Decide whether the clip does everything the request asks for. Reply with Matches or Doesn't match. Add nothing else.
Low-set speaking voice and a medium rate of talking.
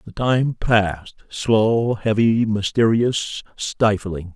Doesn't match